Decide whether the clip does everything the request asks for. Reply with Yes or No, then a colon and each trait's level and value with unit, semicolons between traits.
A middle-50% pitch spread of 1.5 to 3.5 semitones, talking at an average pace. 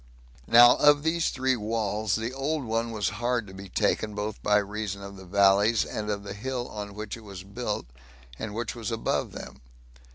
Yes: average, 2.9 semitones; average, 195 wpm